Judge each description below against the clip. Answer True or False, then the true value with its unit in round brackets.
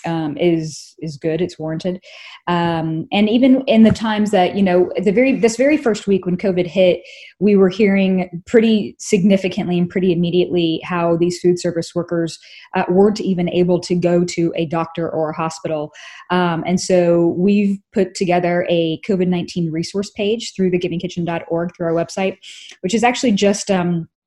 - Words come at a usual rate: True (175 wpm)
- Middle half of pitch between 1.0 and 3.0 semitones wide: True (2.7 semitones)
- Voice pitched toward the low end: False (180 Hz)